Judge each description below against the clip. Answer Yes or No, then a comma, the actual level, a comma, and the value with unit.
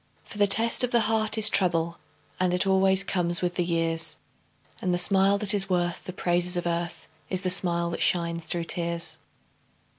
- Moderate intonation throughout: No, narrow, 2.2 semitones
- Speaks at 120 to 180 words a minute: No, average, 190 wpm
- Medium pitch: Yes, medium, 180 Hz